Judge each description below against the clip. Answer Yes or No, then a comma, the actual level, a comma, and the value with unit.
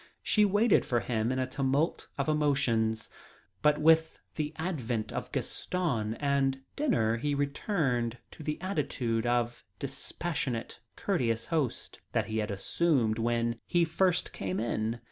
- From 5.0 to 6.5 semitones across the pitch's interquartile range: Yes, average, 5.3 semitones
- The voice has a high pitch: No, low, 130 Hz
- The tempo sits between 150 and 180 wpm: No, average, 140 wpm